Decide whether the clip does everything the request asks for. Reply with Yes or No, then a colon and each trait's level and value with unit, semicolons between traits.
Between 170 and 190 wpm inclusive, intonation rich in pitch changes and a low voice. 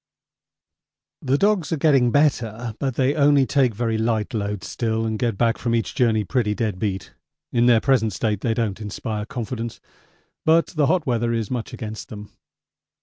No: average, 175 wpm; average, 3.4 semitones; low, 115 Hz